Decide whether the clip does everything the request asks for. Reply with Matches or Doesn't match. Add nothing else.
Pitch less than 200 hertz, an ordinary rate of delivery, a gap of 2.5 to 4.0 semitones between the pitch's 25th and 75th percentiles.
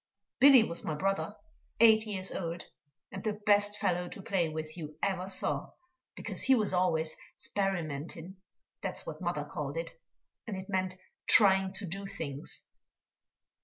Matches